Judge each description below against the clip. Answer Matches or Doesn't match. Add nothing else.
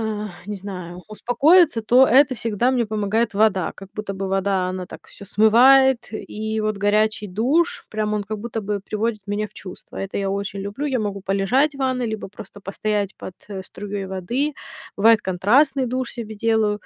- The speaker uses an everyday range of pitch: Matches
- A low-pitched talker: Doesn't match